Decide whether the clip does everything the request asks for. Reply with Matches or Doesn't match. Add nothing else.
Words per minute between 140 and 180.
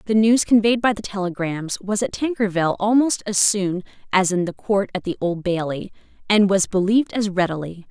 Doesn't match